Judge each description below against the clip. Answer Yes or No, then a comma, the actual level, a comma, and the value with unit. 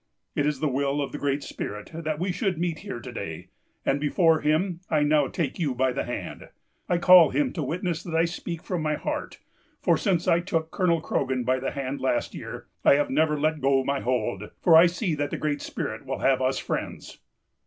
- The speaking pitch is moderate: Yes, medium, 155 Hz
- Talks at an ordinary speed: No, fast, 220 wpm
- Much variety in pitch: No, average, 3.6 semitones